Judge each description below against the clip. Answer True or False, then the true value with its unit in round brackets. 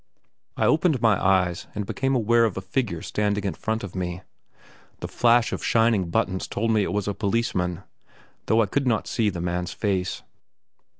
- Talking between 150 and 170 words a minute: False (185 wpm)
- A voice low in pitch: True (105 Hz)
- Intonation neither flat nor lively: True (3.7 semitones)